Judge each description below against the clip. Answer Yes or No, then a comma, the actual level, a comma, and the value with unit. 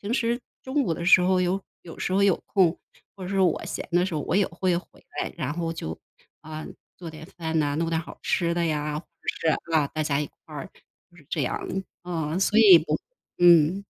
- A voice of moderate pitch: Yes, medium, 170 Hz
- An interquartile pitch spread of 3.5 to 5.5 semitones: No, average, 3.1 semitones